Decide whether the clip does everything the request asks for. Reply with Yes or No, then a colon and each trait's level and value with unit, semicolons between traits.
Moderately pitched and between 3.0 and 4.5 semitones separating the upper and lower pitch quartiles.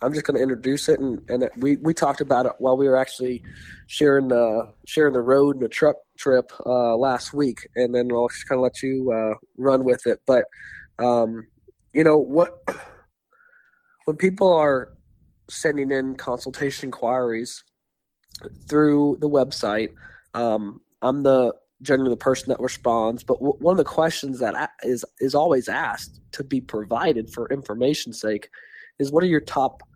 No: low, 130 Hz; average, 3.4 semitones